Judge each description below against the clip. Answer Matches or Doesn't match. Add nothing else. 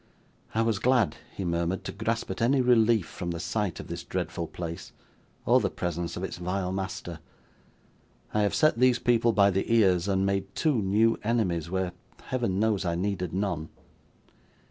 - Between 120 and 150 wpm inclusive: Doesn't match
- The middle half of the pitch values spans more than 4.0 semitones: Matches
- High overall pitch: Doesn't match